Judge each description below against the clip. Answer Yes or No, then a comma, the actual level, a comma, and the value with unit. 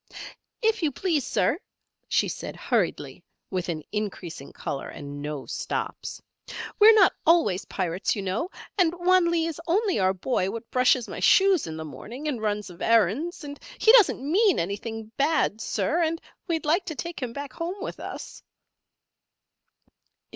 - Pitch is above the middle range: Yes, very high, 270 Hz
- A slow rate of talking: No, average, 160 wpm